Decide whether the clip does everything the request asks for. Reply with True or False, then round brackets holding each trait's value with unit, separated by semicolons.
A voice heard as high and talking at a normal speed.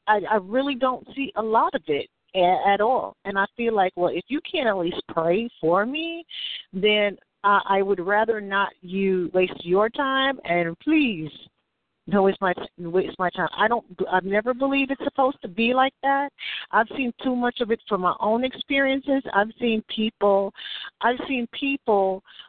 True (215 Hz; 180 wpm)